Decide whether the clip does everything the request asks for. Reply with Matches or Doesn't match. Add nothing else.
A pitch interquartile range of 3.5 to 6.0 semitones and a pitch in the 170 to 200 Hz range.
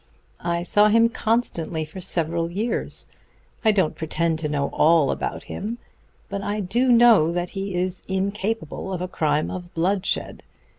Matches